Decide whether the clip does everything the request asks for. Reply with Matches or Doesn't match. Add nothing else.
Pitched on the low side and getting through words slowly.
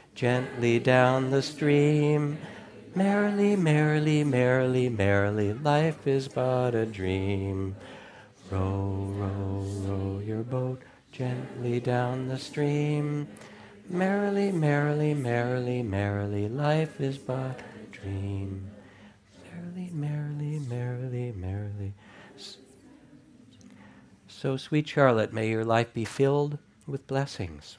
Matches